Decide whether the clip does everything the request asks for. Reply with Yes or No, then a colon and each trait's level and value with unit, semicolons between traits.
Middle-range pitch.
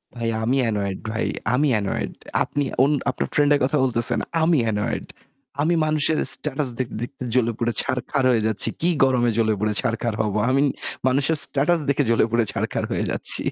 No: low, 125 Hz